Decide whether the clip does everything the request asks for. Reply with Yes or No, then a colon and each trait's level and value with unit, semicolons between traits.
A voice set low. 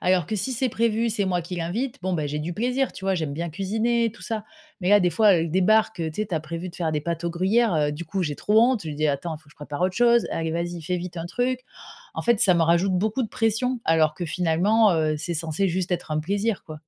No: medium, 180 Hz